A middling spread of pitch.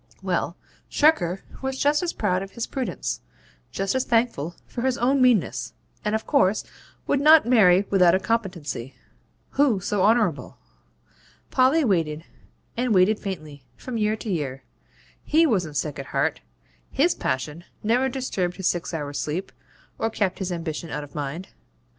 No: wide, 6.7 semitones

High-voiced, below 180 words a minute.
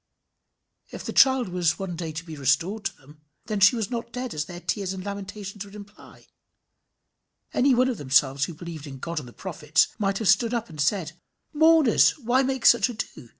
No: high, 195 Hz; average, 200 wpm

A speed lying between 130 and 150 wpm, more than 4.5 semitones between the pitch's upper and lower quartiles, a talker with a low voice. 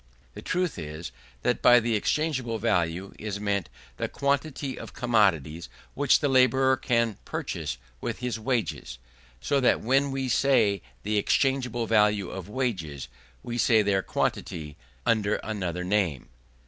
Yes: average, 140 wpm; average, 5.2 semitones; low, 110 Hz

